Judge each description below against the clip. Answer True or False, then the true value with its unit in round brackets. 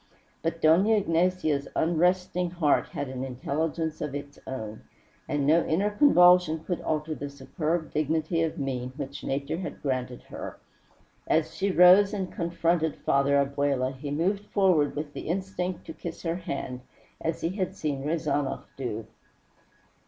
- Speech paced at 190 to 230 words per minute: False (150 wpm)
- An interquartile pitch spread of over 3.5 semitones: True (4.0 semitones)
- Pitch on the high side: False (160 Hz)